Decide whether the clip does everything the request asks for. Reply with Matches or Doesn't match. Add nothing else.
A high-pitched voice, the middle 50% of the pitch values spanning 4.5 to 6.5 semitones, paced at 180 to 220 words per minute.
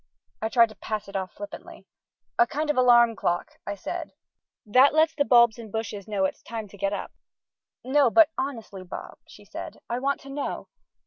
Matches